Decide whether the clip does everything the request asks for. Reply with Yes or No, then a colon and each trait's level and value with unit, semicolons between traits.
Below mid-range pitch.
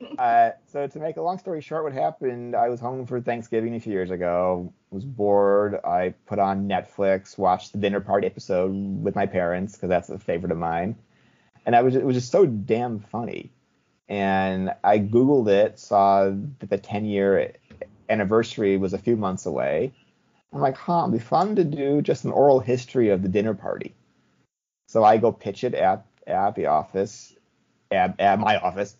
Yes: low, 105 Hz